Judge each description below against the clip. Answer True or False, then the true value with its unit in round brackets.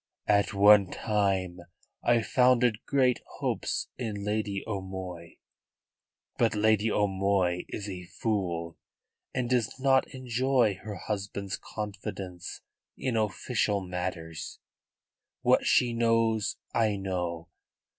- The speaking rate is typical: False (105 wpm)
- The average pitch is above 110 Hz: False (105 Hz)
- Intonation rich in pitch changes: False (3.4 semitones)